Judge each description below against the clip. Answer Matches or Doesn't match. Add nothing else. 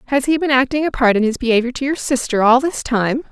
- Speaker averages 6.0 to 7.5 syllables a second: Matches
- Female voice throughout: Matches